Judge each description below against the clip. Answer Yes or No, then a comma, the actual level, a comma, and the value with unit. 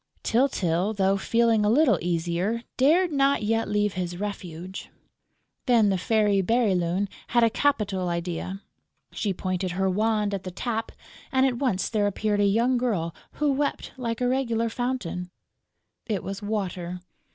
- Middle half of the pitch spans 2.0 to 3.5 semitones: No, average, 4.2 semitones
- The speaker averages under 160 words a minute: Yes, average, 150 wpm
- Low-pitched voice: No, high, 210 Hz